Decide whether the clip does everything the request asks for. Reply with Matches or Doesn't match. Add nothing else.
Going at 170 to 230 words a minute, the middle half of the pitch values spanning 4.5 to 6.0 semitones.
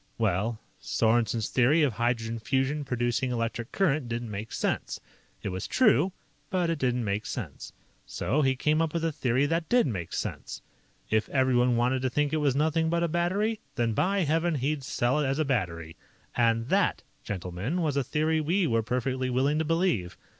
Matches